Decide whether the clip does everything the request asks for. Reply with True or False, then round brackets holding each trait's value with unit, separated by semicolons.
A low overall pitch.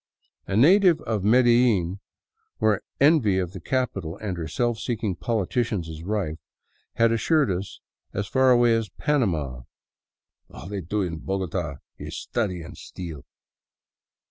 True (105 Hz)